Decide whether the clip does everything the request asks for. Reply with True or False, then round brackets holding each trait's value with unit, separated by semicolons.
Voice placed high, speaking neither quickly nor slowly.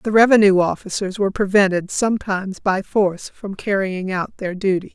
True (195 Hz; 160 wpm)